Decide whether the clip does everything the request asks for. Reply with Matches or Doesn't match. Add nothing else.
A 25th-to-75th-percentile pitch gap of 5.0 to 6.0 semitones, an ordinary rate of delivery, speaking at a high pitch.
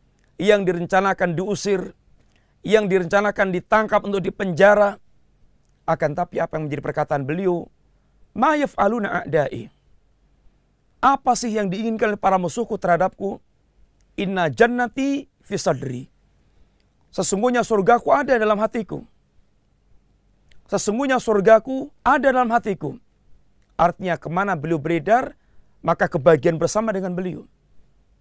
Doesn't match